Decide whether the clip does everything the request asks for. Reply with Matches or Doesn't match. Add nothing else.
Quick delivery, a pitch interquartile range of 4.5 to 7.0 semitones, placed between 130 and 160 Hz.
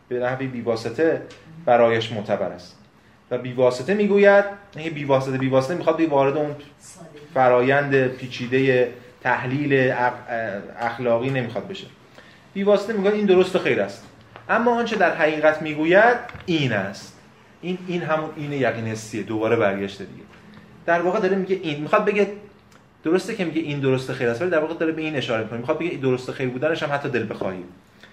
Matches